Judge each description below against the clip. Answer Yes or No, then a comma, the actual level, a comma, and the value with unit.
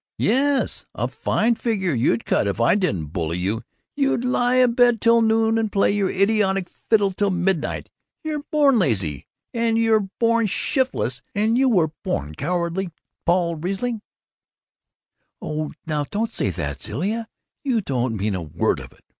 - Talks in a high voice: Yes, high, 195 Hz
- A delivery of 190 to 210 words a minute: No, average, 155 wpm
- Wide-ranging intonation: Yes, wide, 8.1 semitones